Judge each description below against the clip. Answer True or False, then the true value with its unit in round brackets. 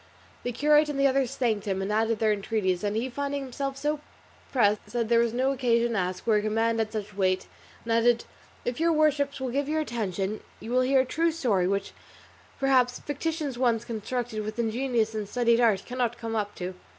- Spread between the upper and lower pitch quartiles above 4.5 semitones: False (3.9 semitones)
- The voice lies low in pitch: False (235 Hz)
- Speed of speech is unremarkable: False (210 wpm)